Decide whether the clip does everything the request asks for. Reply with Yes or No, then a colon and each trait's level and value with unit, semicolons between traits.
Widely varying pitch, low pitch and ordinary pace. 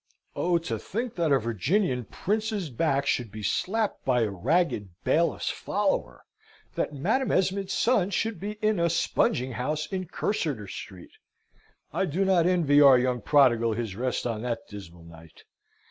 No: wide, 8.2 semitones; medium, 145 Hz; average, 160 wpm